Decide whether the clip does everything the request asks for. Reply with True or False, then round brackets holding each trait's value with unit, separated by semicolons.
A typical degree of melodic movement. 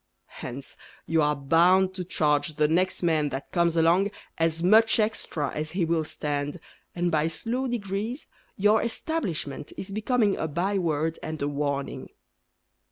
True (4.7 semitones)